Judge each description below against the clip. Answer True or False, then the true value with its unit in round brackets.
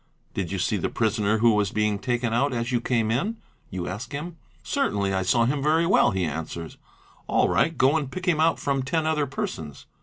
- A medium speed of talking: False (220 wpm)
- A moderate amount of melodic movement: False (6.4 semitones)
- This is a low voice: True (120 Hz)